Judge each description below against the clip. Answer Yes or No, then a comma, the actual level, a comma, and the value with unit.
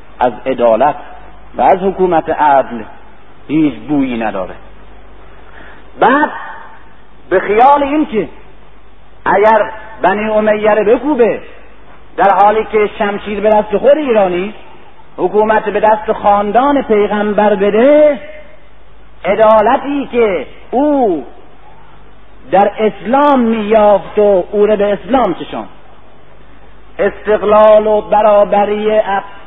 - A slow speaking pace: Yes, slow, 95 wpm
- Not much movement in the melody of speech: Yes, narrow, 2.1 semitones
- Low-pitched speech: No, high, 210 Hz